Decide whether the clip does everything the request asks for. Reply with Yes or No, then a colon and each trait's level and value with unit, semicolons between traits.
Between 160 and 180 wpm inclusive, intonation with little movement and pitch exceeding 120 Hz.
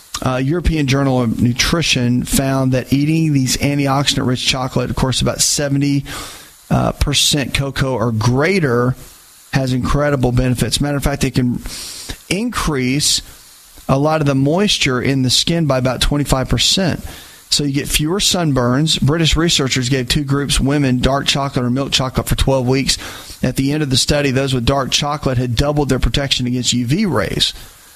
Yes: average, 165 wpm; narrow, 2.2 semitones; low, 135 Hz